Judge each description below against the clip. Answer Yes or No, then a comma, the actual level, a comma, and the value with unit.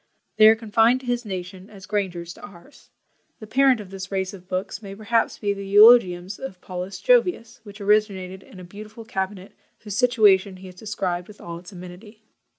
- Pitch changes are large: No, average, 2.8 semitones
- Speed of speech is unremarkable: Yes, average, 190 wpm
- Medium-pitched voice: No, high, 200 Hz